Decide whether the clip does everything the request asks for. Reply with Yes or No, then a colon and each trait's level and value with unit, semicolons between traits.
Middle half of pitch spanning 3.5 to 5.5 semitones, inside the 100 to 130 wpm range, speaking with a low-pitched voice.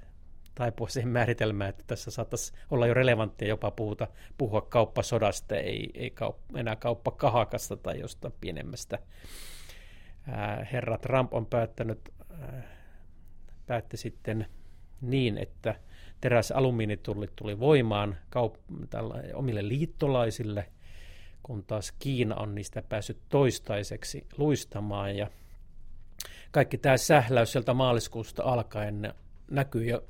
Yes: average, 3.9 semitones; average, 110 wpm; low, 110 Hz